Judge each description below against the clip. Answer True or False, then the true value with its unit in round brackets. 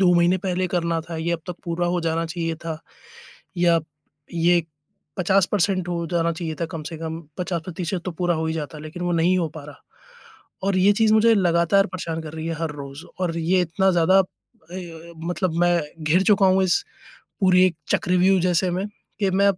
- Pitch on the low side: False (175 Hz)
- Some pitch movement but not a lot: False (2.1 semitones)